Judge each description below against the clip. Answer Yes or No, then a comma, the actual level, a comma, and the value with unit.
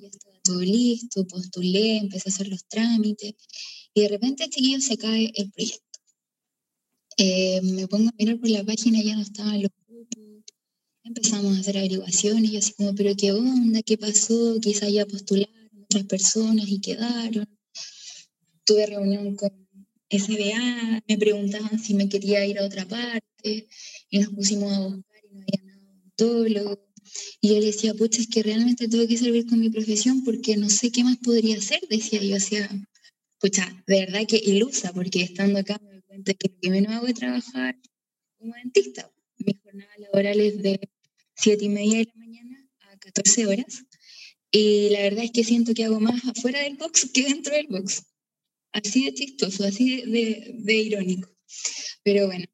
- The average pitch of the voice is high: Yes, high, 210 Hz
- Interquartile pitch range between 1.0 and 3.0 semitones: Yes, narrow, 2.5 semitones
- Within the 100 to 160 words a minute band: No, average, 180 wpm